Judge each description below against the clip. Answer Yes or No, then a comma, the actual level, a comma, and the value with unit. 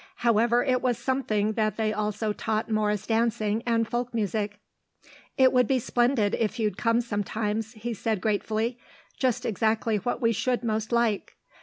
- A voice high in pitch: Yes, high, 225 Hz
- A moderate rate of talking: Yes, average, 160 wpm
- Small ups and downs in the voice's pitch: Yes, narrow, 2.0 semitones